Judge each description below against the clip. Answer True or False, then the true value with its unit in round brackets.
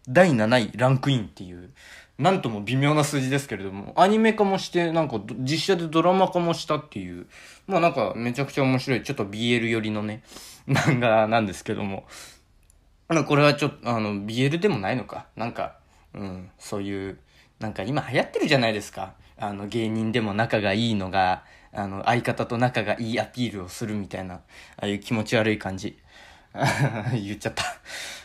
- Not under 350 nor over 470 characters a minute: True (375 characters per minute)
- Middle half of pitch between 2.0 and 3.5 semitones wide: False (5.5 semitones)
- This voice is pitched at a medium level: False (115 Hz)